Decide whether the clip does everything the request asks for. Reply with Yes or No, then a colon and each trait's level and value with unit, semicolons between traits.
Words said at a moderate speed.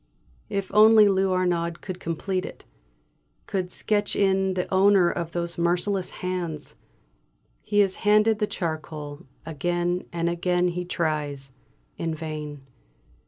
No: slow, 125 wpm